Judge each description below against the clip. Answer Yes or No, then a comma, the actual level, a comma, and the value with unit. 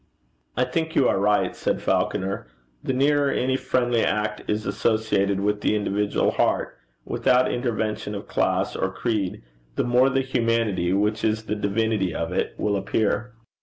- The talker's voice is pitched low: Yes, low, 110 Hz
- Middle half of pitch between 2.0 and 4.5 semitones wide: Yes, average, 3.4 semitones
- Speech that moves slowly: No, average, 160 wpm